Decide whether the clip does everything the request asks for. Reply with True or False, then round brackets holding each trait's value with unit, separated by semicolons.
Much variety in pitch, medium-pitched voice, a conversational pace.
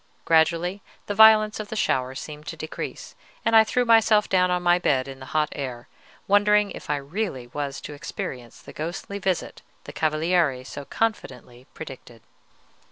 True (6.9 semitones; 160 Hz; 165 wpm)